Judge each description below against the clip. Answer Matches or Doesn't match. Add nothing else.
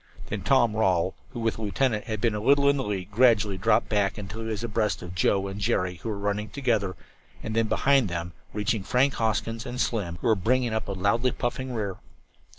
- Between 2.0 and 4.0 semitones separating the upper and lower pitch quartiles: Matches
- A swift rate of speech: Matches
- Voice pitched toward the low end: Matches